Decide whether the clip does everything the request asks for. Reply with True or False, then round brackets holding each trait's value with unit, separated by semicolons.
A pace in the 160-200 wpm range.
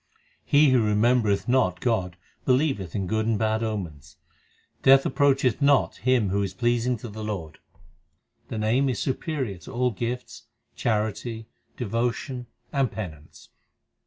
False (135 wpm)